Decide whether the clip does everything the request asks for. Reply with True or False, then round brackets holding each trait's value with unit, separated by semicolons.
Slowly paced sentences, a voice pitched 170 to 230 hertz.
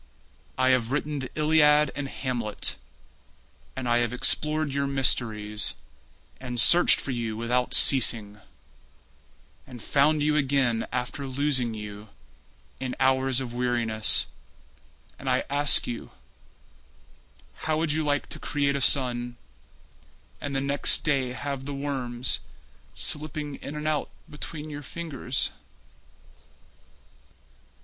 False (120 wpm; 135 Hz)